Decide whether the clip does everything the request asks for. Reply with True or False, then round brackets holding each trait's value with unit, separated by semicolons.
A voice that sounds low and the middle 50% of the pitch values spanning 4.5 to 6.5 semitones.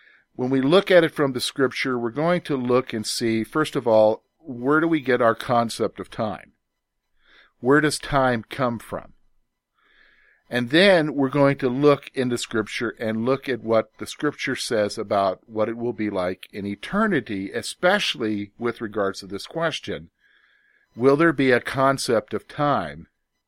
True (125 Hz; 4.9 semitones)